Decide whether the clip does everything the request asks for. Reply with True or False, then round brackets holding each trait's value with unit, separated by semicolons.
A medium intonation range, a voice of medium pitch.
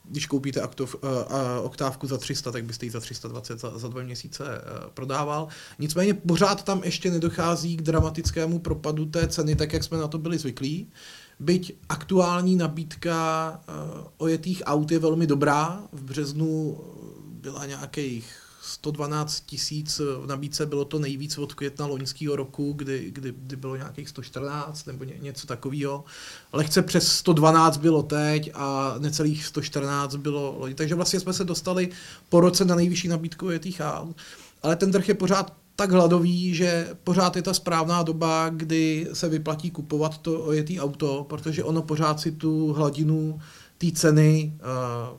True (3.0 semitones; 155 Hz)